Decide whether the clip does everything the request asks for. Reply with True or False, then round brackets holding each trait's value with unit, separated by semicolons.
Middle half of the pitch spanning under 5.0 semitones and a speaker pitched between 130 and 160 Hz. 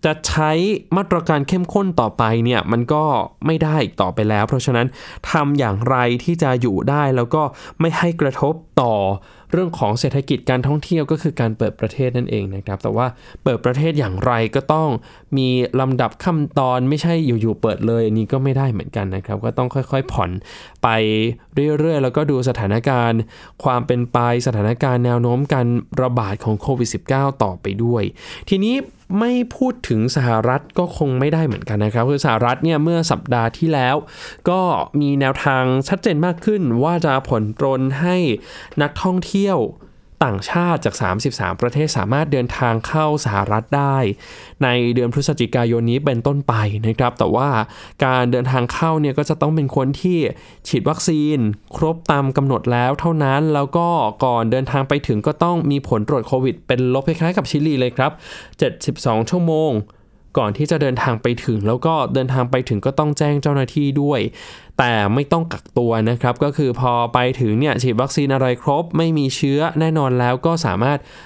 True (4.3 semitones; 135 Hz)